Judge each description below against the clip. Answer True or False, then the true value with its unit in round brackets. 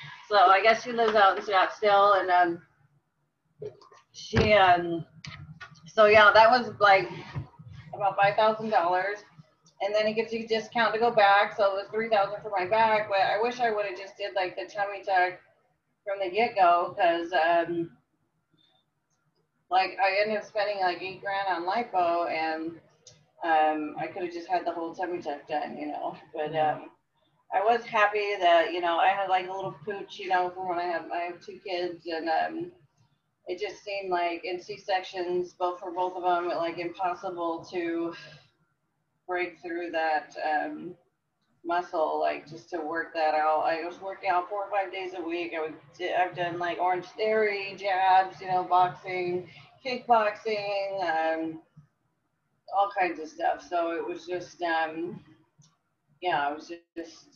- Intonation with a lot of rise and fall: False (3.5 semitones)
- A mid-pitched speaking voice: True (180 Hz)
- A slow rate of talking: False (180 wpm)